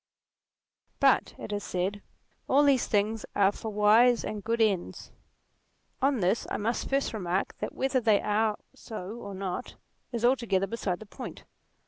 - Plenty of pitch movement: No, average, 2.9 semitones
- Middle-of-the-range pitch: No, high, 215 Hz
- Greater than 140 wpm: Yes, average, 155 wpm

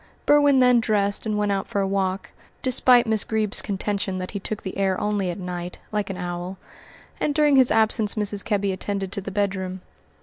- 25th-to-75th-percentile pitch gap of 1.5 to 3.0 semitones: Yes, narrow, 2.4 semitones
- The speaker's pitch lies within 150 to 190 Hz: No, high, 200 Hz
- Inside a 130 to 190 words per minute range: No, average, 200 wpm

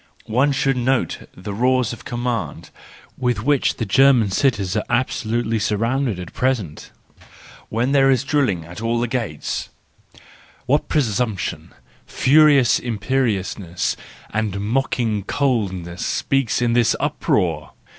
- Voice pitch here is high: No, low, 120 Hz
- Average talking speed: No, slow, 125 wpm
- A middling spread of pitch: Yes, average, 4.5 semitones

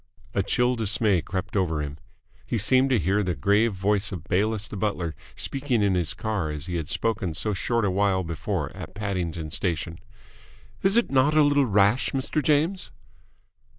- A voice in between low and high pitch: No, low, 100 Hz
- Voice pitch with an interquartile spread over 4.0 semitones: Yes, average, 4.7 semitones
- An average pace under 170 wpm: No, average, 180 wpm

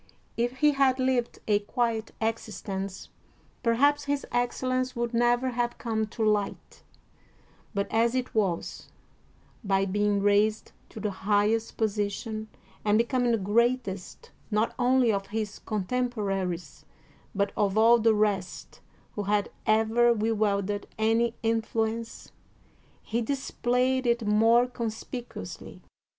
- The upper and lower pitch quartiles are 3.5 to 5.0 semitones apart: No, average, 2.7 semitones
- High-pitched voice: Yes, high, 225 Hz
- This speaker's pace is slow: Yes, slow, 125 wpm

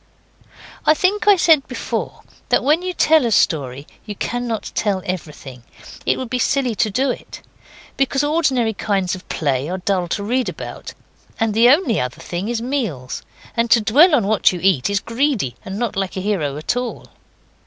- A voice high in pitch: Yes, high, 220 Hz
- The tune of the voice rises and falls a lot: Yes, wide, 6.1 semitones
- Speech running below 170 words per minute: No, average, 185 wpm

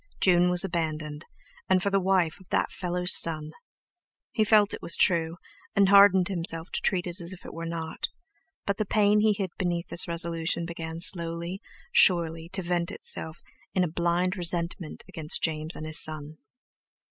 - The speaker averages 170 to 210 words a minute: Yes, average, 175 wpm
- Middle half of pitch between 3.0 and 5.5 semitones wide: No, narrow, 2.4 semitones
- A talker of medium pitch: Yes, medium, 170 Hz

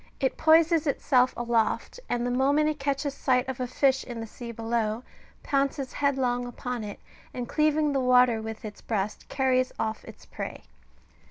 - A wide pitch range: No, average, 2.9 semitones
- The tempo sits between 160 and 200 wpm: Yes, average, 170 wpm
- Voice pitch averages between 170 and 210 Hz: No, very high, 255 Hz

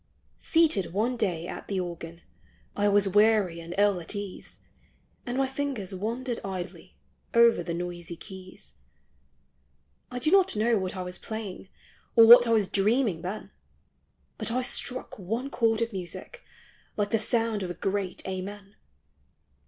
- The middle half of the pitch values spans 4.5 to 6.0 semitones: No, average, 4.0 semitones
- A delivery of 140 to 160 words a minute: Yes, average, 150 wpm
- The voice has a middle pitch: No, high, 205 Hz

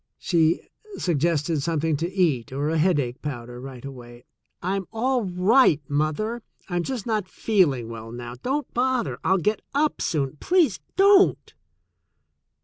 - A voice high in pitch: No, medium, 170 Hz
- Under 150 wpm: Yes, average, 140 wpm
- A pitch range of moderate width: No, wide, 8.0 semitones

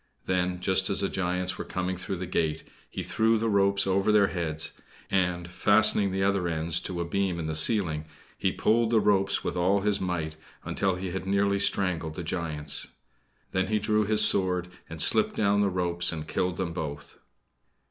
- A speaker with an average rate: Yes, average, 190 wpm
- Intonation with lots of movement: No, narrow, 2.4 semitones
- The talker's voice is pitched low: Yes, very low, 95 Hz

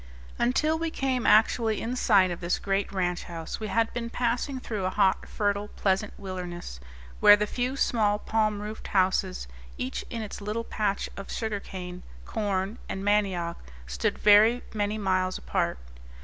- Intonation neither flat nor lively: Yes, average, 3.1 semitones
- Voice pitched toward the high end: Yes, high, 205 Hz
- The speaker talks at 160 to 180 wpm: Yes, average, 165 wpm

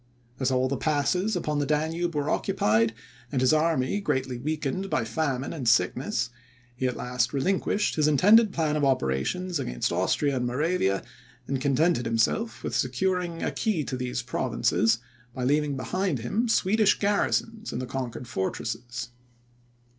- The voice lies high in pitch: No, medium, 140 Hz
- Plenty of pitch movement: Yes, wide, 6.1 semitones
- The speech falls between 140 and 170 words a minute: Yes, average, 155 wpm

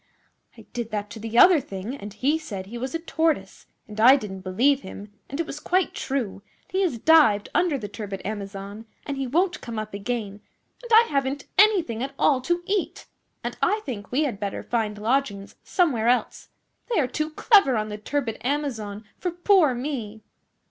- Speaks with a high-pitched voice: Yes, very high, 250 Hz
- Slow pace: No, average, 195 wpm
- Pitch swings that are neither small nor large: No, wide, 6.5 semitones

